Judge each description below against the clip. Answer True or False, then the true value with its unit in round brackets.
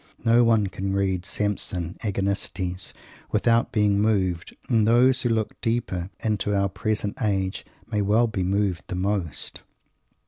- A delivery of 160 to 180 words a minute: False (140 wpm)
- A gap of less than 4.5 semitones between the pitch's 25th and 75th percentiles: True (2.7 semitones)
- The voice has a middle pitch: False (100 Hz)